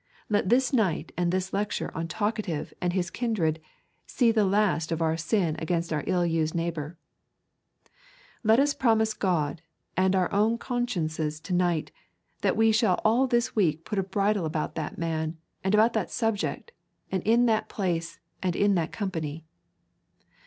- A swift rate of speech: No, average, 165 wpm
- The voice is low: No, medium, 185 Hz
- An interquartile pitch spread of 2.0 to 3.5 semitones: No, average, 4.8 semitones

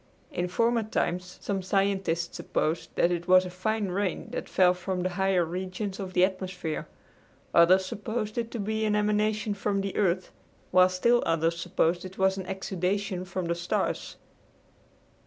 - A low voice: No, medium, 185 Hz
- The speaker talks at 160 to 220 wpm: Yes, average, 165 wpm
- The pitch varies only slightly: Yes, narrow, 2.3 semitones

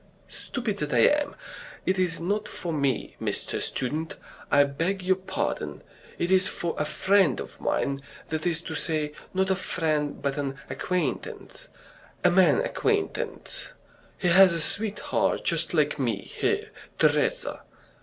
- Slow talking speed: No, average, 145 wpm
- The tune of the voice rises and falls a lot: No, average, 4.4 semitones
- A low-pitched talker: No, medium, 175 Hz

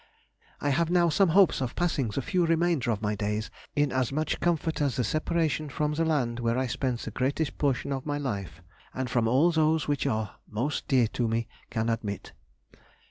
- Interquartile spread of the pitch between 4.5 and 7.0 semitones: Yes, average, 5.1 semitones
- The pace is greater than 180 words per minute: Yes, average, 200 wpm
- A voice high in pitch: No, low, 135 Hz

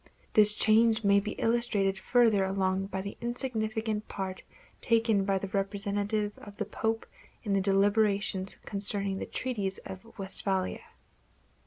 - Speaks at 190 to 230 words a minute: No, slow, 135 wpm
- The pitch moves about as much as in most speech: No, narrow, 2.1 semitones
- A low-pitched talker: No, high, 205 Hz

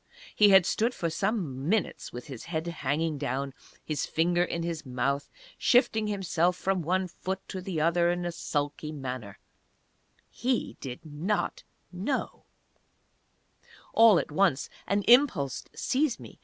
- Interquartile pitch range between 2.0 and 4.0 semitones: No, average, 5.0 semitones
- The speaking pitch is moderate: Yes, medium, 170 Hz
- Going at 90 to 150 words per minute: Yes, average, 140 wpm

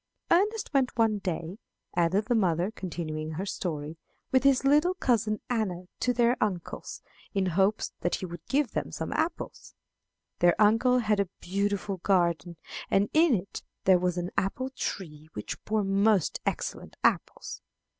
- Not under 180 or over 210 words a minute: No, average, 155 wpm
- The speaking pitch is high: Yes, high, 200 Hz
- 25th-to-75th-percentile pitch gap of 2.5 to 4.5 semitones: No, average, 5.3 semitones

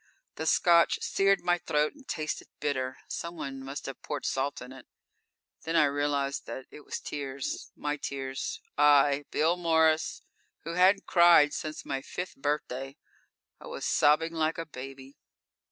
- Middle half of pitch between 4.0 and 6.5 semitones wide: No, average, 3.1 semitones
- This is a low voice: No, medium, 150 Hz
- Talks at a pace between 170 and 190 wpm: No, average, 155 wpm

